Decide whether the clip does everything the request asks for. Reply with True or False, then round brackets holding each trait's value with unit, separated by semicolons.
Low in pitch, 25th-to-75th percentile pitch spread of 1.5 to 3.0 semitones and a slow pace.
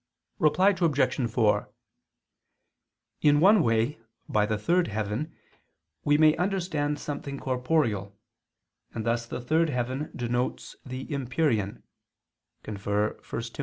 False (130 Hz; 5.4 semitones; 110 wpm)